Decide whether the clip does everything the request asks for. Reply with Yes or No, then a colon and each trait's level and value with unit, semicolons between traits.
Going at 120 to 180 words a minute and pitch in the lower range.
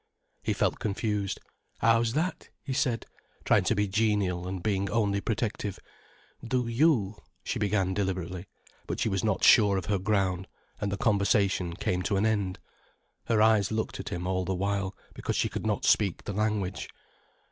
Yes: average, 170 wpm; low, 100 Hz